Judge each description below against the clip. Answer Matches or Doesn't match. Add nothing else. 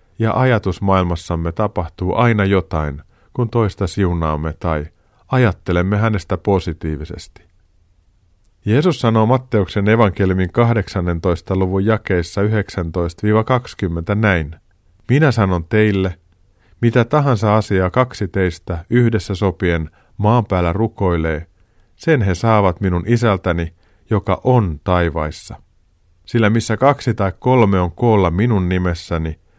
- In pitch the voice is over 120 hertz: Doesn't match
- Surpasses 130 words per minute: Doesn't match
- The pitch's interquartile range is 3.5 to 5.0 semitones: Matches